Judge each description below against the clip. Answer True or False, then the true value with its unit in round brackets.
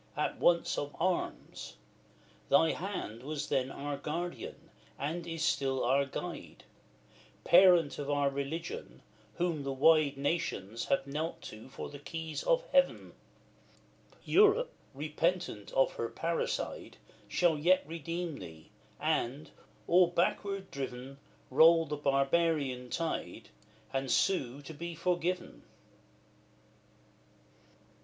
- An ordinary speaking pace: False (115 wpm)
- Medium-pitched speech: True (155 Hz)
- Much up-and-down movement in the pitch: False (3.9 semitones)